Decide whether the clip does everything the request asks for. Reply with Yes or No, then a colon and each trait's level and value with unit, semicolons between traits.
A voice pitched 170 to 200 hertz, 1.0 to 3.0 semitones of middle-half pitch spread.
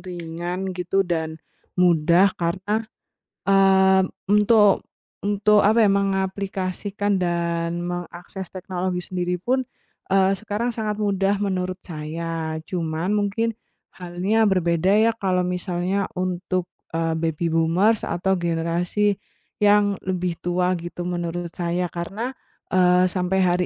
Yes: medium, 185 Hz; narrow, 2.4 semitones